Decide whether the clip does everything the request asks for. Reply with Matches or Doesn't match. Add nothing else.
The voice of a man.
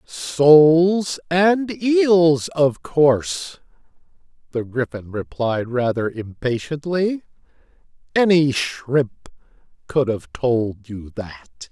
Matches